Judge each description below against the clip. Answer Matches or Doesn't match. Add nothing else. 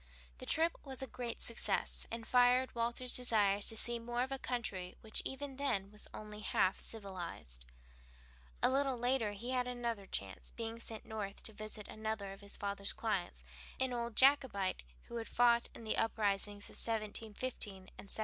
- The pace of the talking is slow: Doesn't match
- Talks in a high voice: Matches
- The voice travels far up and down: Doesn't match